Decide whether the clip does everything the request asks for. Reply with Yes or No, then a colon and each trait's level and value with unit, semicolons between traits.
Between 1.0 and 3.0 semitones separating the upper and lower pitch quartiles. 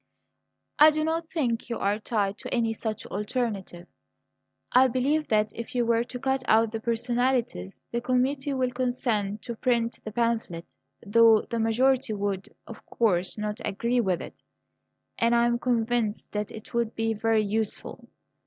Yes: average, 2.7 semitones